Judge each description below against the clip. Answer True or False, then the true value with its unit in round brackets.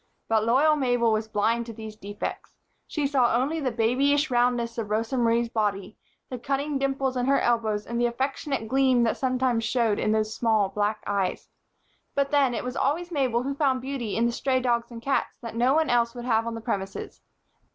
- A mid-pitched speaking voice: False (240 Hz)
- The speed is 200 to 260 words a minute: True (205 wpm)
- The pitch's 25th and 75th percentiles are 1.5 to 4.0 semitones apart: True (3.1 semitones)